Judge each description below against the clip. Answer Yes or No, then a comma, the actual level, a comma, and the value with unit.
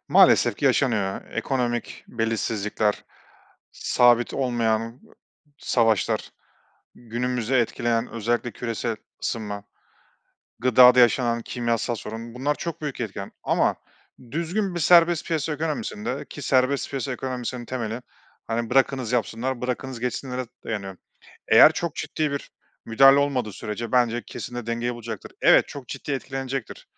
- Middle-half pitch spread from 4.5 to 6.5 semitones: No, average, 2.7 semitones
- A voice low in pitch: Yes, low, 120 Hz